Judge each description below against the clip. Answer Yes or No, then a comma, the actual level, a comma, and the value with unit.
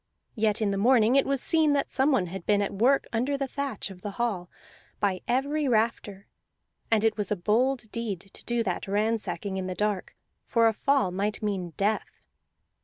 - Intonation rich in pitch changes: No, average, 4.3 semitones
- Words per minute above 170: Yes, average, 190 wpm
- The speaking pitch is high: Yes, high, 215 Hz